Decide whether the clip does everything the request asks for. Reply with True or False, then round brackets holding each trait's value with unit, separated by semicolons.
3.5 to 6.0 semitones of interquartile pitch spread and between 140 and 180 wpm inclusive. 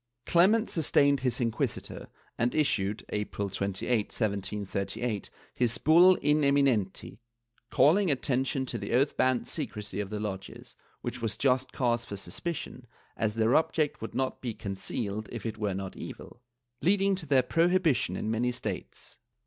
True (5.3 semitones; 150 wpm)